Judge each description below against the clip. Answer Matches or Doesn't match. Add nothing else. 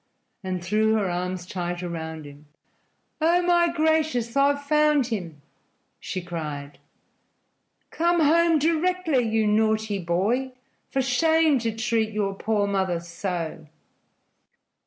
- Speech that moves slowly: Matches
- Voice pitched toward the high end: Matches